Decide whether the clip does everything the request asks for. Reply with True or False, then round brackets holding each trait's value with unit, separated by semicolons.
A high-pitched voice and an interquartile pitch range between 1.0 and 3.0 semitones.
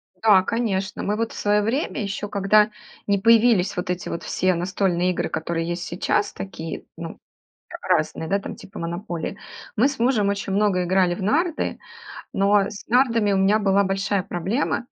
True (200 Hz; 2.7 semitones)